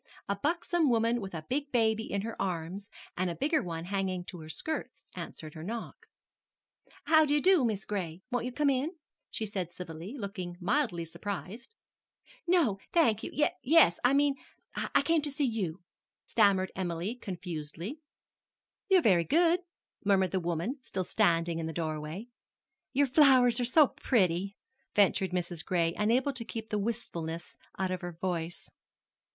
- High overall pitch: Yes, high, 200 Hz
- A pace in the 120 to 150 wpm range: No, average, 160 wpm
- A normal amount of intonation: No, wide, 6.8 semitones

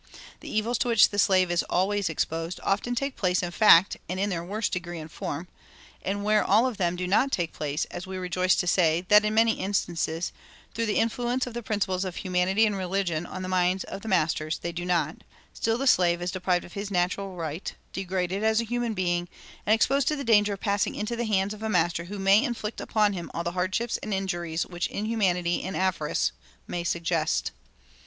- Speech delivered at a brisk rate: Yes, fast, 215 wpm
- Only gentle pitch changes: No, average, 3.4 semitones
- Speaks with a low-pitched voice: No, high, 190 Hz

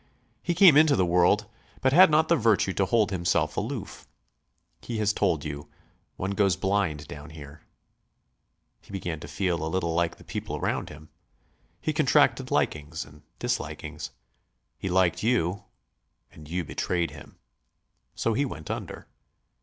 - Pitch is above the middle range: No, very low, 90 Hz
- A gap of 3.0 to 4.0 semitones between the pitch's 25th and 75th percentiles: No, average, 5.1 semitones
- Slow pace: No, average, 155 wpm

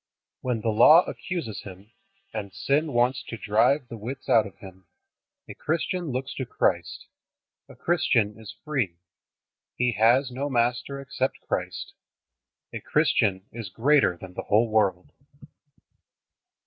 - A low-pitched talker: Yes, low, 120 Hz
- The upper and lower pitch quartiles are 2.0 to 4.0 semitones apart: No, average, 4.9 semitones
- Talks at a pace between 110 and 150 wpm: Yes, slow, 135 wpm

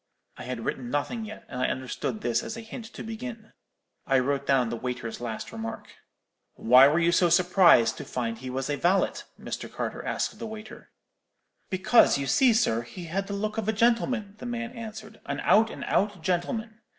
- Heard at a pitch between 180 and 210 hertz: Yes, medium, 185 Hz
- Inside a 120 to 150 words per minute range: No, average, 200 wpm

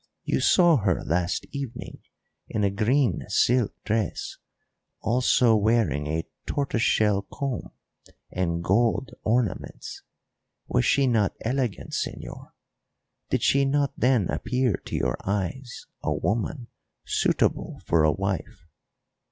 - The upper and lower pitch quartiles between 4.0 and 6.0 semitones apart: Yes, average, 4.7 semitones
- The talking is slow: Yes, slow, 120 wpm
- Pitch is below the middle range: Yes, low, 115 Hz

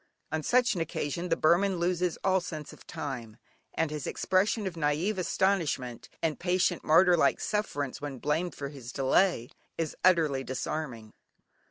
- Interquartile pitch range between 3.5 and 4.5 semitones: Yes, average, 4.2 semitones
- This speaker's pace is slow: No, average, 155 wpm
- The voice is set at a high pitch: No, medium, 165 Hz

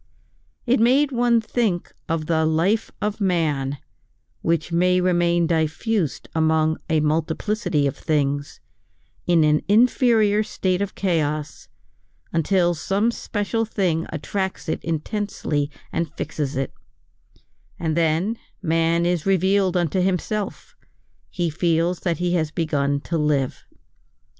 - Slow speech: Yes, slow, 120 wpm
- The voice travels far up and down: No, average, 3.9 semitones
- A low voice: No, medium, 170 Hz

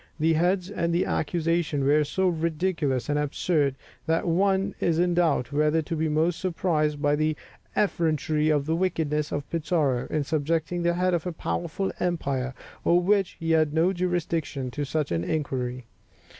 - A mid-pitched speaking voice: Yes, medium, 160 Hz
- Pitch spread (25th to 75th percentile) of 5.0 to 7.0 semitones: No, average, 2.8 semitones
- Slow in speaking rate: No, average, 170 wpm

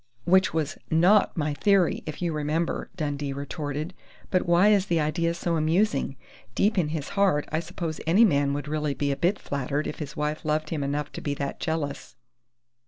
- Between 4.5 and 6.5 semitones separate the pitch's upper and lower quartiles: No, average, 3.0 semitones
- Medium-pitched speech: Yes, medium, 155 Hz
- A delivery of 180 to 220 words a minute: Yes, average, 190 wpm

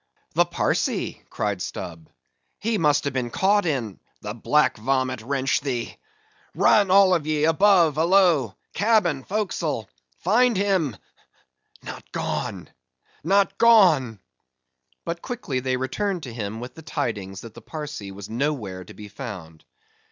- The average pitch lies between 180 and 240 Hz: No, medium, 145 Hz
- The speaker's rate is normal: No, slow, 120 wpm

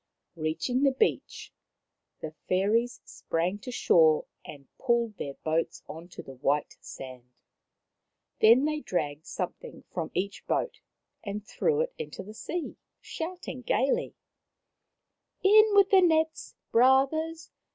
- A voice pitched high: Yes, high, 230 Hz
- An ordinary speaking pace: No, slow, 130 wpm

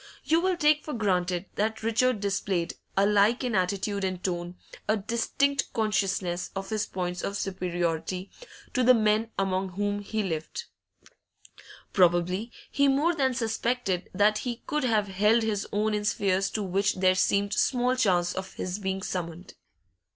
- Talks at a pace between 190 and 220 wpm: No, average, 155 wpm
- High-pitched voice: Yes, high, 200 Hz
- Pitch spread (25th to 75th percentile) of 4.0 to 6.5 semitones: No, average, 3.5 semitones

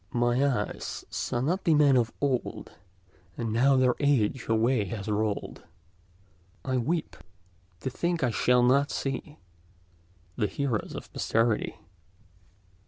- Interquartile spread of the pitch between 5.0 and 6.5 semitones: No, average, 4.2 semitones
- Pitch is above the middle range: No, low, 125 Hz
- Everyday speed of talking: No, slow, 120 wpm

